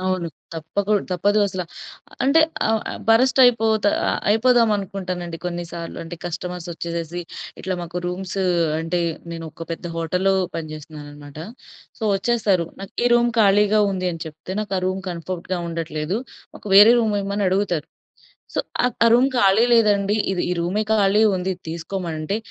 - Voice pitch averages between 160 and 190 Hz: Yes, medium, 185 Hz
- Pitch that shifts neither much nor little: Yes, average, 3.7 semitones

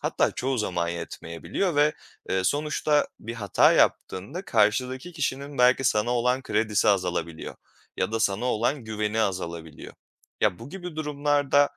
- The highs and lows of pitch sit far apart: Yes, wide, 6.5 semitones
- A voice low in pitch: Yes, low, 120 Hz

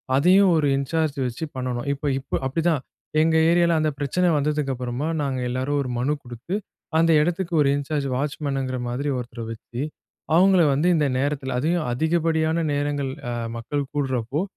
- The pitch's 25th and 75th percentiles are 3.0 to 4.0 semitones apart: Yes, average, 3.7 semitones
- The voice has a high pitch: No, medium, 145 Hz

